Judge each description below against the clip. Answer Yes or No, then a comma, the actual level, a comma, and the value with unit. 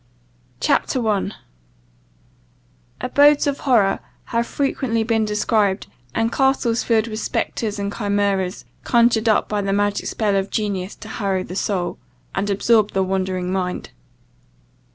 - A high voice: Yes, high, 210 Hz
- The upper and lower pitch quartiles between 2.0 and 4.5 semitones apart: Yes, average, 2.9 semitones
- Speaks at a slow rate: Yes, slow, 130 wpm